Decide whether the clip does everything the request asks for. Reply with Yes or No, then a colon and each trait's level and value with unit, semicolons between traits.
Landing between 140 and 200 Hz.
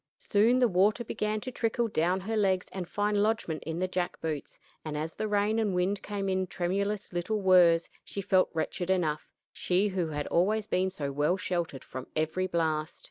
Yes: medium, 185 Hz